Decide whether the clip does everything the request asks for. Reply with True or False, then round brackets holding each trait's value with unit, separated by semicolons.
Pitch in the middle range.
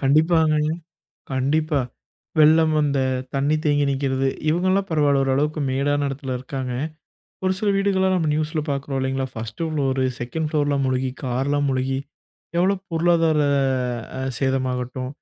True (145 Hz)